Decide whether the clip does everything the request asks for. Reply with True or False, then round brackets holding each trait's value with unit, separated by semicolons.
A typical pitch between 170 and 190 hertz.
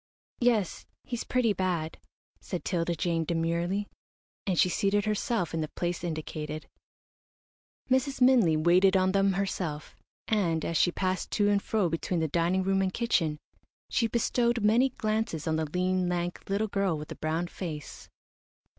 True (185 Hz)